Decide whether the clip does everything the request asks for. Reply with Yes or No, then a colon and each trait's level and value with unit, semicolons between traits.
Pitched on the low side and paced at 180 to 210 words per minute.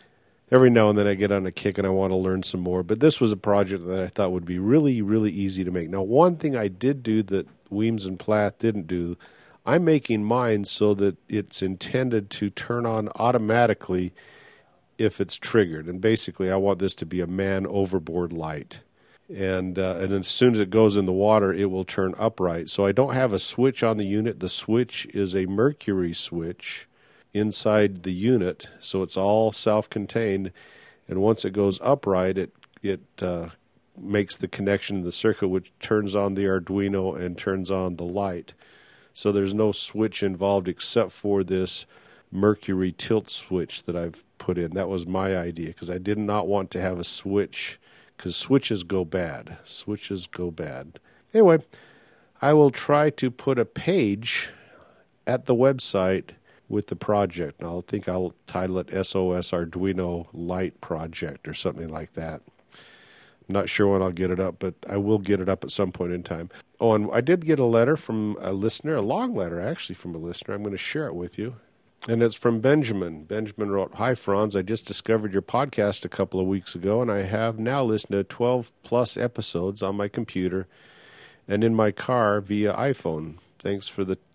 Yes: low, 100 Hz; average, 195 wpm